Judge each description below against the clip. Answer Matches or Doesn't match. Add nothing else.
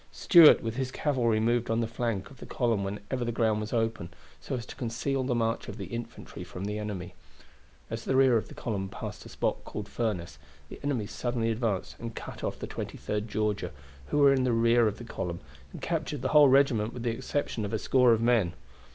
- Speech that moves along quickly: Matches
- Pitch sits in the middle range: Doesn't match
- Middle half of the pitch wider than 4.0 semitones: Doesn't match